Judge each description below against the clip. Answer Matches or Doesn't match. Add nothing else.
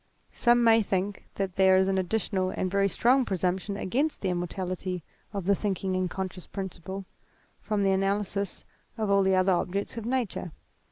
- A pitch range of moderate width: Doesn't match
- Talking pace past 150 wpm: Matches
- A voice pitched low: Doesn't match